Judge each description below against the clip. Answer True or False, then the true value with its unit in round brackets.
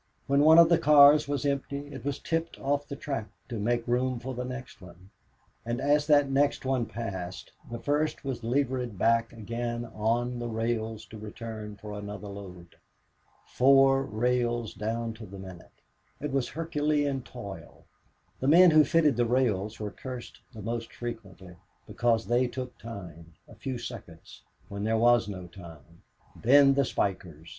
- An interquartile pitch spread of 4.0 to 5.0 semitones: True (4.4 semitones)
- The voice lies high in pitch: False (120 Hz)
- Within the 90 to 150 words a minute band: False (165 wpm)